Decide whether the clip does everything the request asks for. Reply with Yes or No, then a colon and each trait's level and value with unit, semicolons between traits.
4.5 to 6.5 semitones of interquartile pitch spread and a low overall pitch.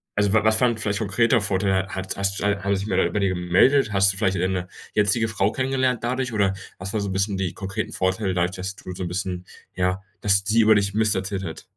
No: narrow, 2.4 semitones; low, 100 Hz